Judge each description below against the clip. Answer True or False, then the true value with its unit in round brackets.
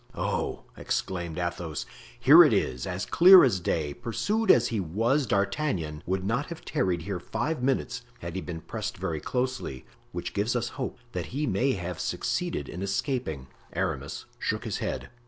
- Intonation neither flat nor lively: False (7.0 semitones)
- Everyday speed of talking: True (170 wpm)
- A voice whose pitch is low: True (100 Hz)